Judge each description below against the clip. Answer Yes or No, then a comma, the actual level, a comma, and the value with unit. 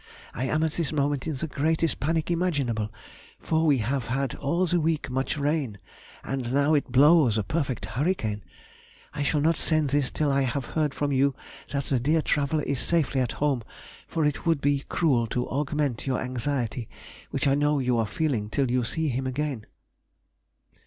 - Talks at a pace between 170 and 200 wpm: Yes, average, 185 wpm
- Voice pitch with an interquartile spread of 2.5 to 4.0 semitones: Yes, average, 3.3 semitones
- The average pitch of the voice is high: No, medium, 140 Hz